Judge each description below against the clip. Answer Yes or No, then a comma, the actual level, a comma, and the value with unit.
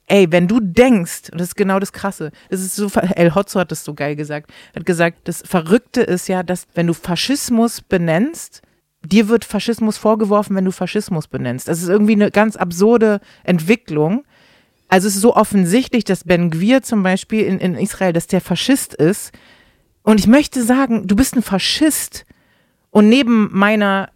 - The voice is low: No, high, 200 Hz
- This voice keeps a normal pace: Yes, average, 180 wpm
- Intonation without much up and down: No, average, 3.8 semitones